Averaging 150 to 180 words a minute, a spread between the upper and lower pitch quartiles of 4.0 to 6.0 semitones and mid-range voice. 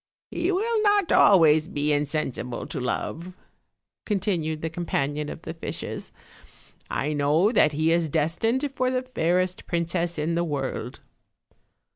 No: slow, 135 wpm; average, 4.8 semitones; medium, 165 Hz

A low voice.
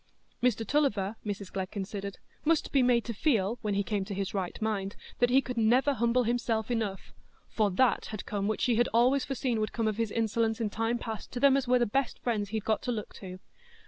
No: high, 225 Hz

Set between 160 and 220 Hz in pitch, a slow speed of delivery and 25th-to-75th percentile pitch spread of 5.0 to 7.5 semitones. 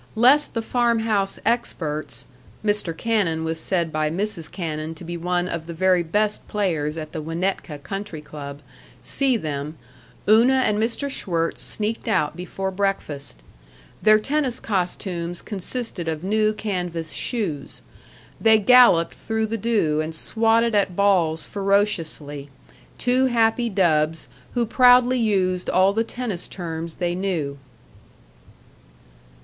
Yes: high, 190 Hz; slow, 130 wpm; wide, 5.4 semitones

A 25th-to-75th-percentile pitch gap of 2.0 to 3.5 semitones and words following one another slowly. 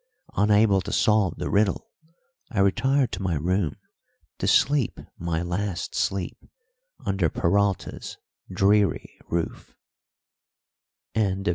Yes: average, 2.8 semitones; slow, 100 wpm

